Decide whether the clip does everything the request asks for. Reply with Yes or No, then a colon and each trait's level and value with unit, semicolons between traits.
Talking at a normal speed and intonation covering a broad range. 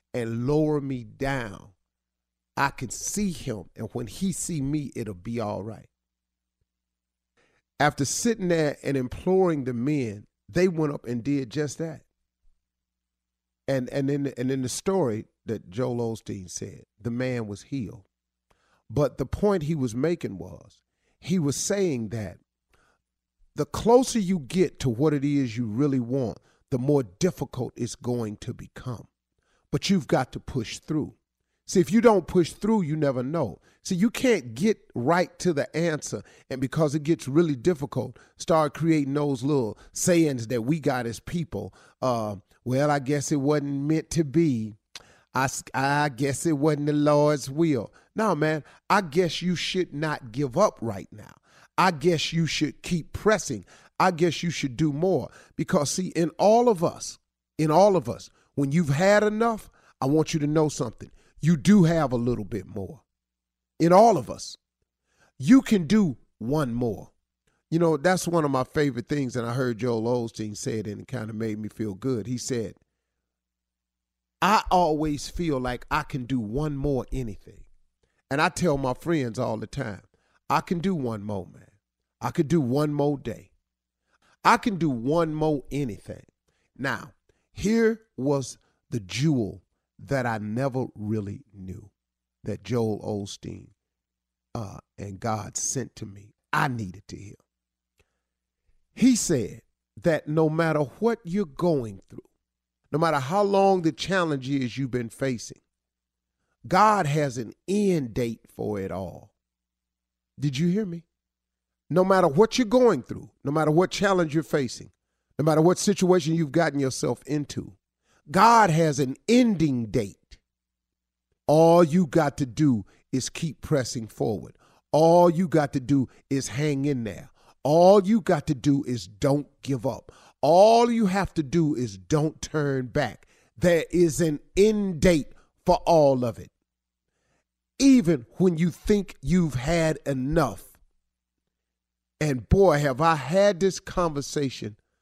Yes: average, 160 wpm; wide, 7.3 semitones